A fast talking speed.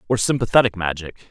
No: average, 140 wpm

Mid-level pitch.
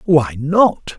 Yes: medium, 160 Hz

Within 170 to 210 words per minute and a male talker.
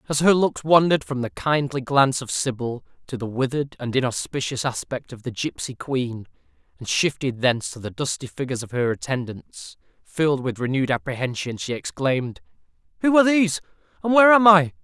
Yes: average, 175 wpm; male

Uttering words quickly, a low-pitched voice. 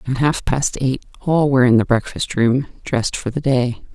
Yes: fast, 215 wpm; low, 130 Hz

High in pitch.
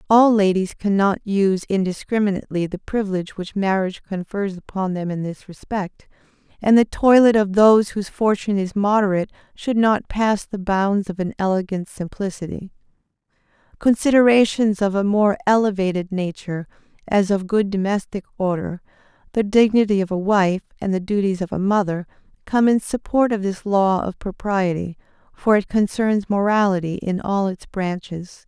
Yes: high, 200 Hz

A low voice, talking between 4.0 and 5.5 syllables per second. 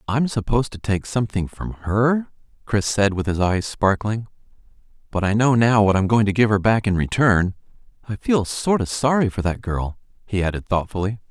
Yes: low, 105 Hz; 5.2 syllables/s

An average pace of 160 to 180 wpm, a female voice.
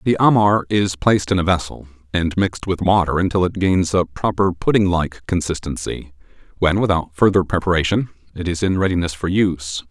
No: average, 175 wpm; male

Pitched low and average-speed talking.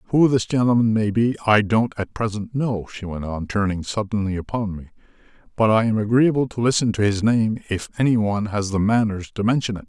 No: low, 110 Hz; fast, 215 wpm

